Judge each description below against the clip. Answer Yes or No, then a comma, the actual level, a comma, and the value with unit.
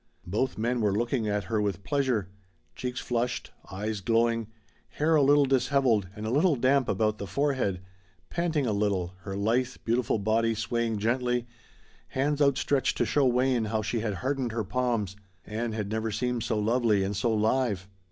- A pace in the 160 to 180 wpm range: Yes, average, 170 wpm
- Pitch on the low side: Yes, low, 115 Hz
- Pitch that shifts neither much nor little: Yes, average, 3.4 semitones